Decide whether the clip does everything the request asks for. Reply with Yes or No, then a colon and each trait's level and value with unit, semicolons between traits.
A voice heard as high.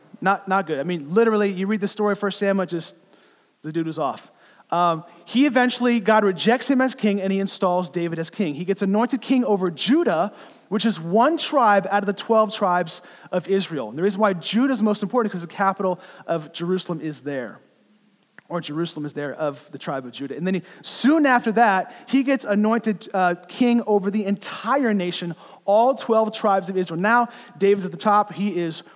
Yes: high, 195 Hz